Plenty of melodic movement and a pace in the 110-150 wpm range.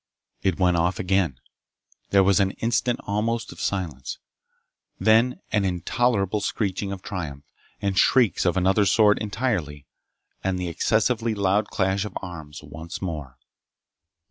No: average, 3.3 semitones; slow, 135 wpm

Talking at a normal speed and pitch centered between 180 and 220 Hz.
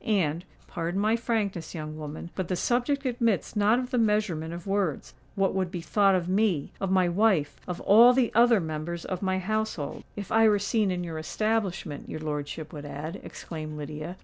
Yes: average, 175 wpm; medium, 185 Hz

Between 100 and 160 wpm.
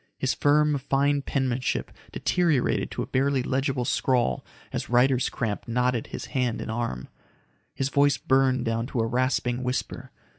Yes: average, 150 wpm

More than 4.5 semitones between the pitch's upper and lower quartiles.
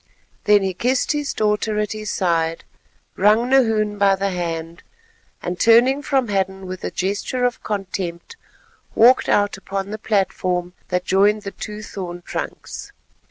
No: average, 2.9 semitones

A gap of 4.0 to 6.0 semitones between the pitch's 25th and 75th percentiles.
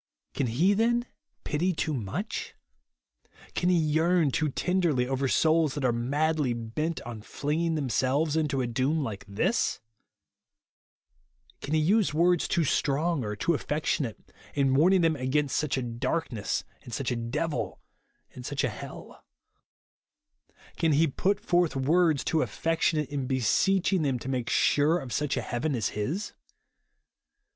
Yes: average, 4.3 semitones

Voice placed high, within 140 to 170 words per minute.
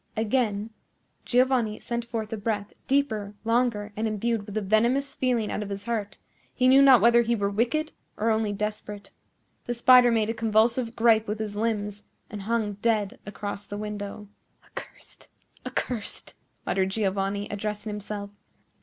Yes: high, 215 Hz; average, 155 wpm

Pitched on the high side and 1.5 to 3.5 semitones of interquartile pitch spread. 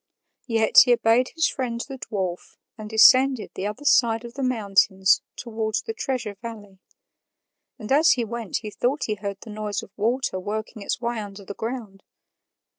Yes: high, 225 Hz; average, 3.2 semitones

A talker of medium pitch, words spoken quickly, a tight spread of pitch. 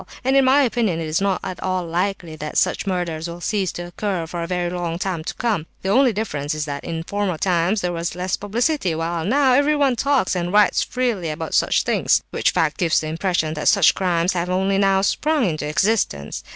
No: medium, 180 Hz; fast, 215 wpm; average, 3.9 semitones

